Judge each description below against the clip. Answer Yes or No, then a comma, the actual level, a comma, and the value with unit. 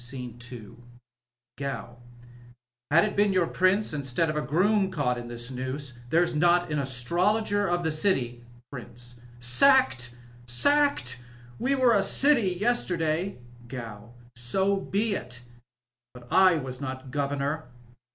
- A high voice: No, medium, 140 Hz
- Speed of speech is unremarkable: Yes, average, 145 wpm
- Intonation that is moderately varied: No, wide, 7.5 semitones